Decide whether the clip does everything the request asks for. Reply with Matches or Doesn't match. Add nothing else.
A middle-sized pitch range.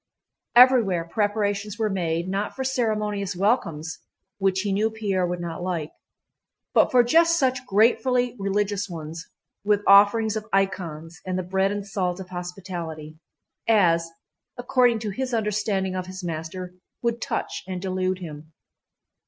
Matches